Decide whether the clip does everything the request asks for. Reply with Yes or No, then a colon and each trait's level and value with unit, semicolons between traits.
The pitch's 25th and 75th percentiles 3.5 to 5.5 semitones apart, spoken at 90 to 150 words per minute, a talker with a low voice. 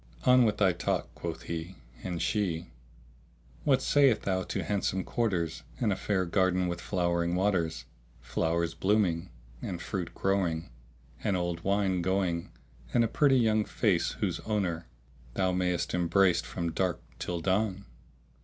No: average, 3.0 semitones; average, 145 wpm; very low, 90 Hz